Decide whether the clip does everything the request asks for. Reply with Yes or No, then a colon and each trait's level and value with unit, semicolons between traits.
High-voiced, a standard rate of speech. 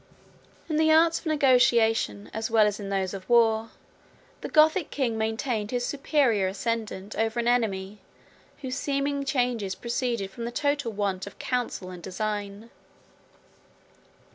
Yes: high, 230 Hz; average, 145 wpm